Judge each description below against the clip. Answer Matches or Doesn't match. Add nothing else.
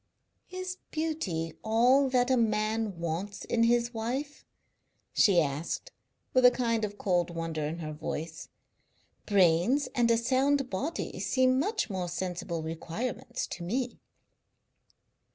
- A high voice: Matches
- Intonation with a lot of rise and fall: Matches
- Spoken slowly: Matches